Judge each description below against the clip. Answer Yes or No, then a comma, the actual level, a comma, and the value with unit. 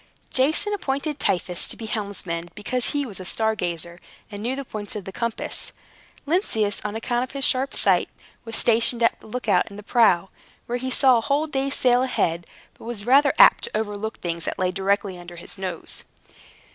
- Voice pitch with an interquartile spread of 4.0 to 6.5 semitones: Yes, average, 5.2 semitones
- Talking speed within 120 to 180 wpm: No, average, 200 wpm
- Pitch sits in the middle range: No, high, 225 Hz